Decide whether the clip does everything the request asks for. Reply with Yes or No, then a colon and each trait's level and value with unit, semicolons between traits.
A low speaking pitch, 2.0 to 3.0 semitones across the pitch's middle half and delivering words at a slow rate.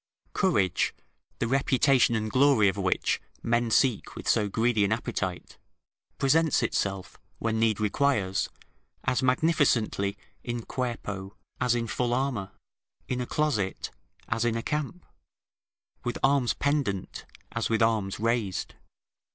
No: low, 115 Hz; average, 4.2 semitones; slow, 125 wpm